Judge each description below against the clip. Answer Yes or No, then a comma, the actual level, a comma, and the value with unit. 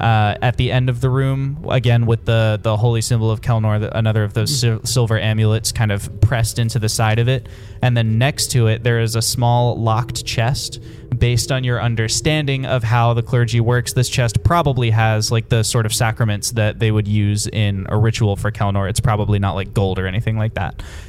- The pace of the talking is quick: Yes, fast, 220 wpm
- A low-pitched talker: Yes, low, 115 Hz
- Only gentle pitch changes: Yes, narrow, 1.9 semitones